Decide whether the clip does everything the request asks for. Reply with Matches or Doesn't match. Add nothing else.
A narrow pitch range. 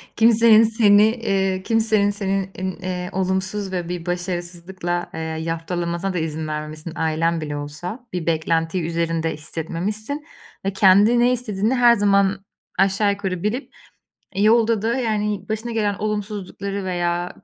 Doesn't match